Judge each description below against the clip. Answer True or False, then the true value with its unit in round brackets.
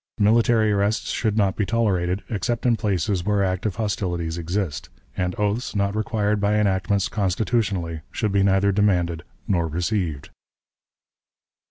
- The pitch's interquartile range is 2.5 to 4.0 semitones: True (2.8 semitones)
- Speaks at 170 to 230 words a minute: False (135 wpm)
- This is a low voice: True (100 Hz)